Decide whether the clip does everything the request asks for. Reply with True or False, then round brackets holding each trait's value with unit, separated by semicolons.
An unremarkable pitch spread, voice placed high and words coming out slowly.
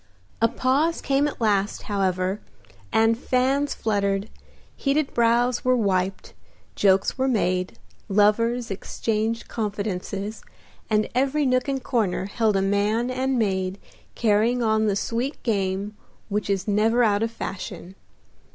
True (3.7 semitones; 220 Hz; 130 wpm)